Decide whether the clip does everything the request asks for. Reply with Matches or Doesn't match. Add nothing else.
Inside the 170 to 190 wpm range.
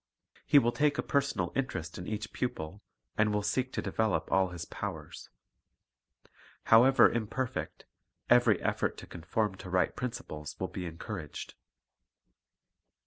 Doesn't match